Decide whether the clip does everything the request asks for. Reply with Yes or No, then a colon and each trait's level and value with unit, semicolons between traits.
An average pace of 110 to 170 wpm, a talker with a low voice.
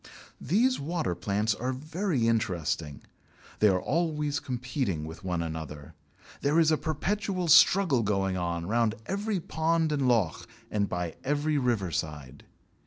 Yes: average, 140 wpm; low, 120 Hz